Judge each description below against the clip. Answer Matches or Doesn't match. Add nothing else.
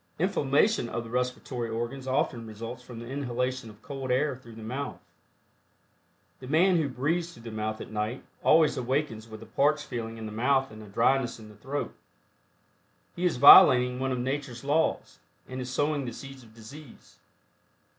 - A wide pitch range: Doesn't match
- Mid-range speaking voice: Doesn't match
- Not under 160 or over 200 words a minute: Matches